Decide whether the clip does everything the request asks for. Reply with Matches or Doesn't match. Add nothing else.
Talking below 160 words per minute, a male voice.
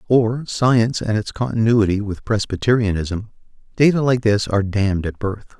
Matches